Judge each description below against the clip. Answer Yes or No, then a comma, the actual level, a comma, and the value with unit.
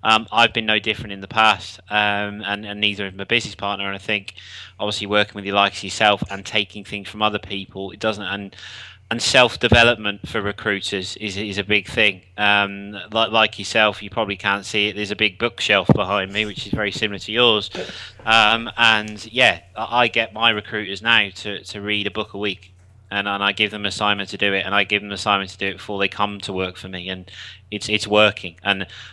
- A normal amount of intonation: No, narrow, 1.4 semitones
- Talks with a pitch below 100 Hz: No, low, 105 Hz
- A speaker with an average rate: No, fast, 225 wpm